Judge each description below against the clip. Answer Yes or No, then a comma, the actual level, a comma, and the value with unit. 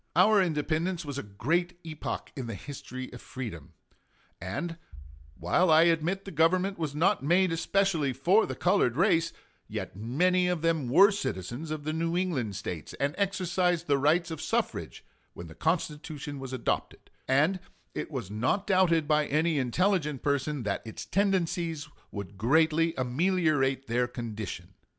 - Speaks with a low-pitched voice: No, medium, 155 Hz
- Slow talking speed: No, average, 155 wpm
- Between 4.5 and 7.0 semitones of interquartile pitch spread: Yes, wide, 5.4 semitones